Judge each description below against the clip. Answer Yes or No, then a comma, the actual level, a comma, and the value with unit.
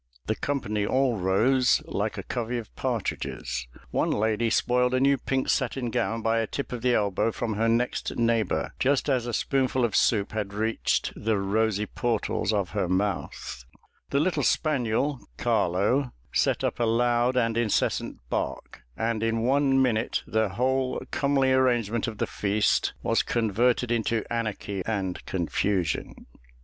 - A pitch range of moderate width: Yes, average, 3.1 semitones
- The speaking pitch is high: No, low, 115 Hz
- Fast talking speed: No, average, 155 wpm